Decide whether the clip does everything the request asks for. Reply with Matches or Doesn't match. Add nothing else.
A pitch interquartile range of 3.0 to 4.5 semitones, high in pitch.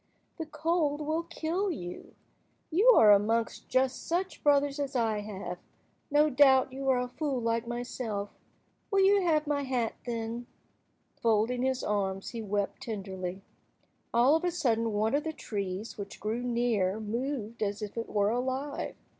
Doesn't match